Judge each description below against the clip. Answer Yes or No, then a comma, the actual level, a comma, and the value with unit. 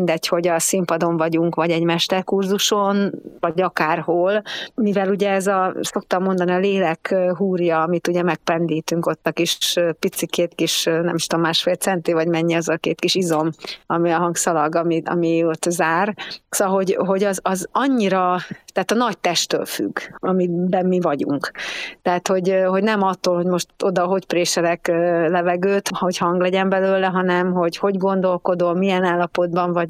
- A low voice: No, medium, 180 Hz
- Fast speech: Yes, fast, 165 wpm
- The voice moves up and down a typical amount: No, narrow, 2.1 semitones